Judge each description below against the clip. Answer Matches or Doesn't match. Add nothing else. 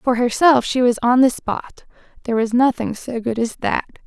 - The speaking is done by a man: Doesn't match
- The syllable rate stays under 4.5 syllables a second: Doesn't match